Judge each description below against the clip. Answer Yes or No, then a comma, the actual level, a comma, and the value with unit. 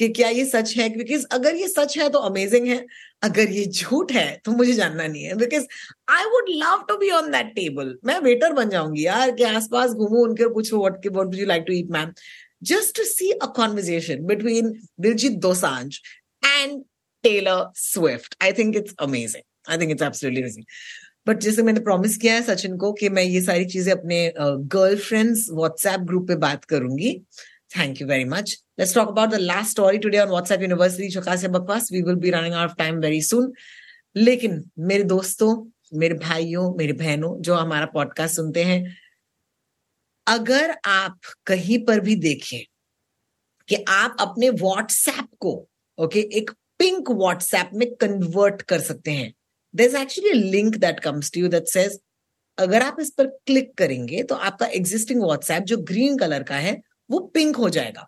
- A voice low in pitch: No, high, 200 Hz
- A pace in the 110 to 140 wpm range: No, average, 155 wpm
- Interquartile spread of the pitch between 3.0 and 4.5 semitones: No, wide, 5.4 semitones